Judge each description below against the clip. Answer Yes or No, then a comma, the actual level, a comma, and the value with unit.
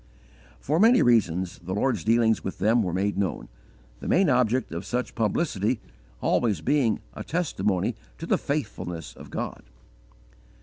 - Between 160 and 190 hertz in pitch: No, low, 110 Hz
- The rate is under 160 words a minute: Yes, average, 145 wpm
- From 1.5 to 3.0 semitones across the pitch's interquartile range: No, wide, 5.4 semitones